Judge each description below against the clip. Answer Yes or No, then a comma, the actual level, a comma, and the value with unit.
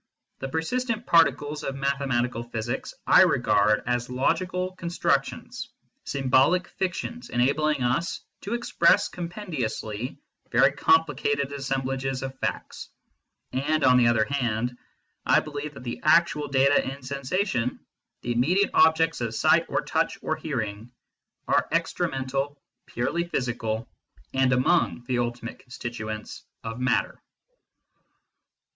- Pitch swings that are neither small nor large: Yes, average, 4.8 semitones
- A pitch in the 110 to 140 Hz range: Yes, low, 135 Hz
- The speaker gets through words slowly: Yes, slow, 120 wpm